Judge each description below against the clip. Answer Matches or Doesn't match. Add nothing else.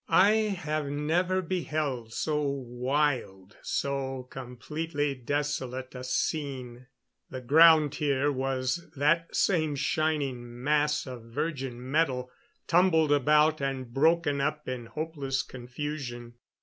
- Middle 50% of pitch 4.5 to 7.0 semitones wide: Doesn't match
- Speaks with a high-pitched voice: Doesn't match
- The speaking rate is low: Matches